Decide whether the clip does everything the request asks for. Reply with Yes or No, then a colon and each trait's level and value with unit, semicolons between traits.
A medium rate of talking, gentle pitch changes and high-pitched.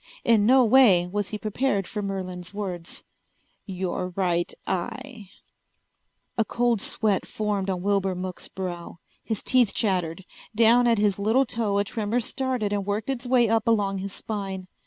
No: average, 155 wpm; average, 3.3 semitones; high, 205 Hz